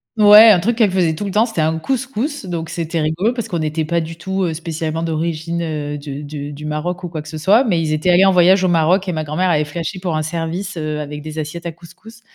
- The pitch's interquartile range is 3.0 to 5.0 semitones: Yes, average, 3.5 semitones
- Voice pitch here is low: No, medium, 170 Hz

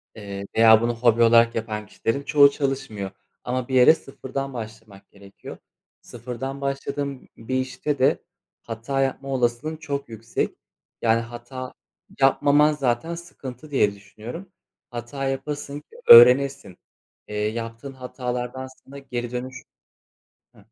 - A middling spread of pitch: Yes, average, 3.2 semitones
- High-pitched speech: No, low, 125 Hz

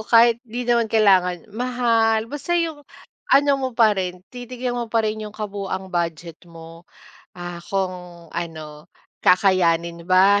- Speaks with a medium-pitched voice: No, high, 195 Hz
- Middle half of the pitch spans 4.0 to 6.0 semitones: Yes, average, 5.2 semitones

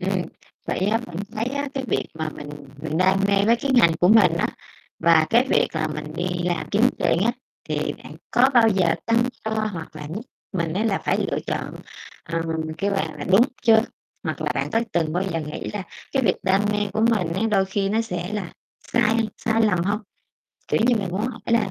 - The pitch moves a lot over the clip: No, average, 4.4 semitones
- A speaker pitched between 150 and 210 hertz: Yes, high, 200 Hz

